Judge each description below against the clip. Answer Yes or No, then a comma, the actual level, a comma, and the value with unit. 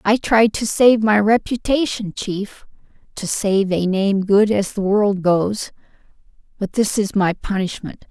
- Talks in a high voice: Yes, high, 205 Hz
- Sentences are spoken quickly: No, average, 150 wpm